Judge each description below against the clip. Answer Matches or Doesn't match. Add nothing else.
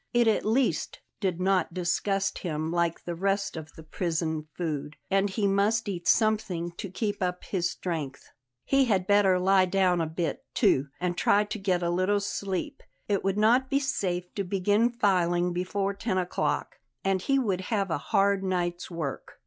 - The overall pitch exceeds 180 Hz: Matches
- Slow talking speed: Doesn't match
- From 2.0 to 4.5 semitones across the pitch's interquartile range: Matches